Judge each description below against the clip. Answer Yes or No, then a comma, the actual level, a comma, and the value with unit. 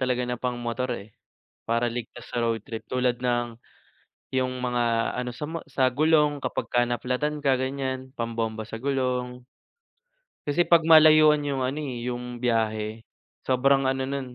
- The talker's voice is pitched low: Yes, low, 125 Hz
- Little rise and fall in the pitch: Yes, narrow, 2.3 semitones